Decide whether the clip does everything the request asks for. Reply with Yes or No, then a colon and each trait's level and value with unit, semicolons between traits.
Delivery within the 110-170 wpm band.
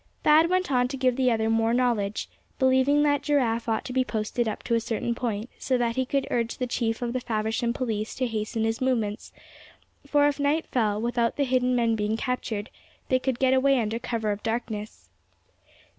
No: fast, 205 wpm